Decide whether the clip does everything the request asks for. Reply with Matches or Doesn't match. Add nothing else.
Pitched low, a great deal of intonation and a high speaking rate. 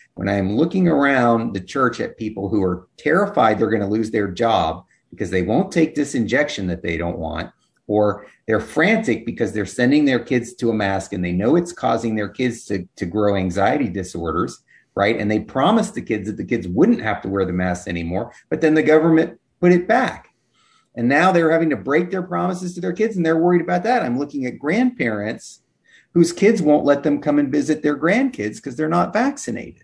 Matches